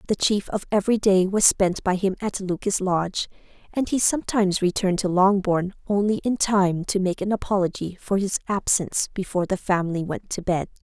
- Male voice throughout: No, female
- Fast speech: No, average, 185 wpm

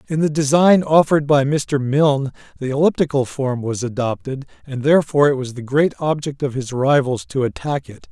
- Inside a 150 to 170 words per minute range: No, average, 185 wpm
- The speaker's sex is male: Yes, male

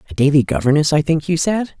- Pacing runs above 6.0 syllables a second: Yes, 6.4 syllables/s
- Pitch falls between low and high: Yes, medium, 150 Hz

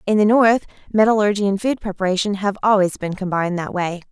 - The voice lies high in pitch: Yes, high, 200 Hz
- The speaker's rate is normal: Yes, average, 190 wpm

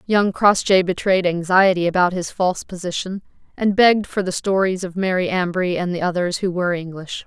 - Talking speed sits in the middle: Yes, average, 180 wpm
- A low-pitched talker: No, medium, 185 Hz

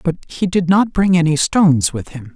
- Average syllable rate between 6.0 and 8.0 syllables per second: No, 5.1 syllables/s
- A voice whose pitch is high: No, medium, 170 Hz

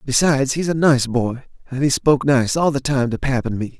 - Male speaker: Yes, male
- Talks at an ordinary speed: No, fast, 255 wpm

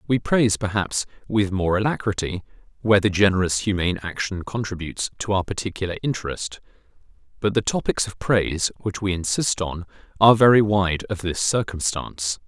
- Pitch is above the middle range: No, low, 100 Hz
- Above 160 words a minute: No, average, 150 wpm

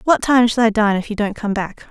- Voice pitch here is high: Yes, high, 220 Hz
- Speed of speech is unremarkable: No, fast, 345 wpm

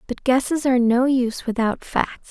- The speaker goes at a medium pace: Yes, average, 180 wpm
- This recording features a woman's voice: Yes, female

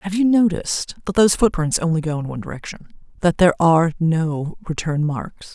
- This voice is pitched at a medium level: Yes, medium, 165 Hz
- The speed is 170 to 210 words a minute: Yes, average, 175 wpm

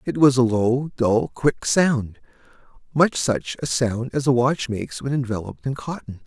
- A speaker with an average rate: Yes, average, 170 wpm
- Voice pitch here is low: Yes, low, 125 Hz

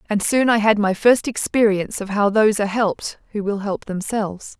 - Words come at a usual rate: No, fast, 210 wpm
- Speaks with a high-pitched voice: Yes, high, 210 Hz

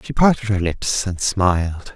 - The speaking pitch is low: Yes, low, 100 Hz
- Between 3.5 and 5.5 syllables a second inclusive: Yes, 4.3 syllables/s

